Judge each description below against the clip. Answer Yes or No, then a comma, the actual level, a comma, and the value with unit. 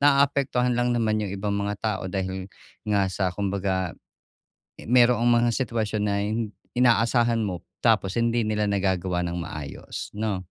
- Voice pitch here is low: Yes, low, 105 Hz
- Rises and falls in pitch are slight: No, average, 3.7 semitones